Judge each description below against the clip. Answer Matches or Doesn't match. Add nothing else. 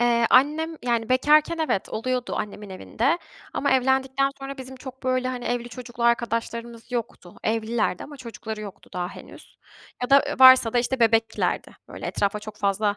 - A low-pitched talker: Doesn't match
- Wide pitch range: Doesn't match